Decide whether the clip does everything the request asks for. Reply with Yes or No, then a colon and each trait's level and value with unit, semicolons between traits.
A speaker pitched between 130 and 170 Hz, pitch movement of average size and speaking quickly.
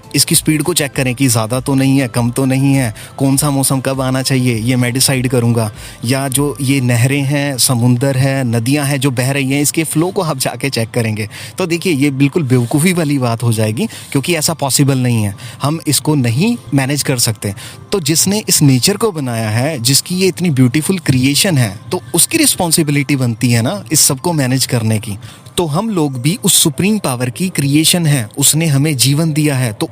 Yes: medium, 140 Hz; average, 3.4 semitones; fast, 210 wpm